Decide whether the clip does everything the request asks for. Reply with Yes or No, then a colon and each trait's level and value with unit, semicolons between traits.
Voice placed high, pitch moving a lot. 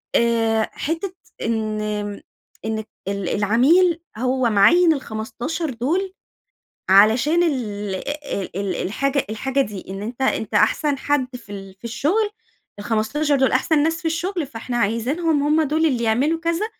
Yes: very high, 255 Hz; wide, 6.3 semitones